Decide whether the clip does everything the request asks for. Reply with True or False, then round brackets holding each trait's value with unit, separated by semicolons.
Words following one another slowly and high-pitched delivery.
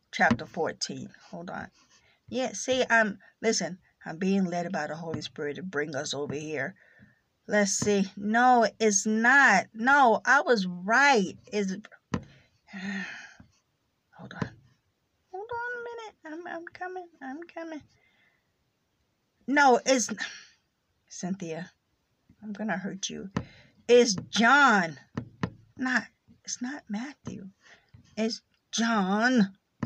True (115 wpm; 220 Hz)